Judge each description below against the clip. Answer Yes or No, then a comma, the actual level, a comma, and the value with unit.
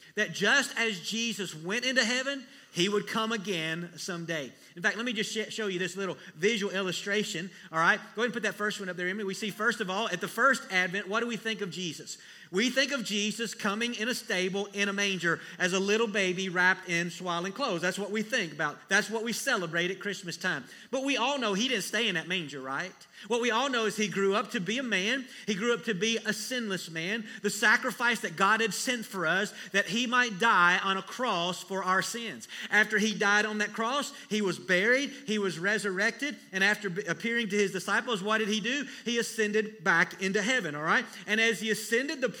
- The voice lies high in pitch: Yes, high, 210 Hz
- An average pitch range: Yes, average, 3.4 semitones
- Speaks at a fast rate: Yes, fast, 235 wpm